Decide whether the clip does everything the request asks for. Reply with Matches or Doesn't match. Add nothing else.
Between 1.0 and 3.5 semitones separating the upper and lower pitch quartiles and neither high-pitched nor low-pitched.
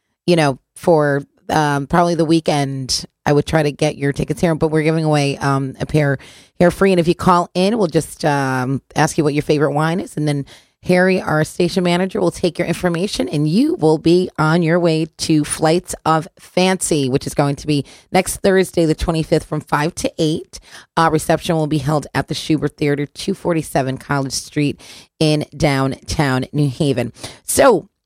Matches